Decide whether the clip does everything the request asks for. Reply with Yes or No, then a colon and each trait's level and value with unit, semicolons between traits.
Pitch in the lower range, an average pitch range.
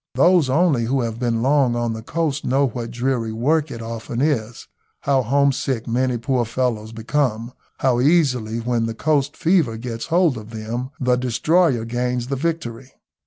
Yes: low, 125 Hz; average, 3.4 semitones